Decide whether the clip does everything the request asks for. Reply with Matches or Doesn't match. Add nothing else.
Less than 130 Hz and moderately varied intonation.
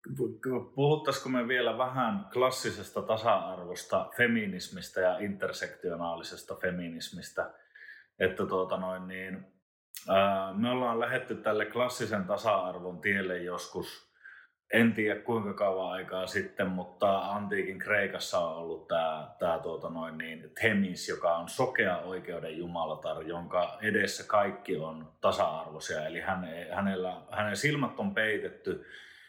Doesn't match